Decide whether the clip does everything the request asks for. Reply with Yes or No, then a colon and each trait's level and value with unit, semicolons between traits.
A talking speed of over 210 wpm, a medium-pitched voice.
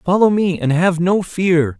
No: average, 200 wpm; medium, 175 Hz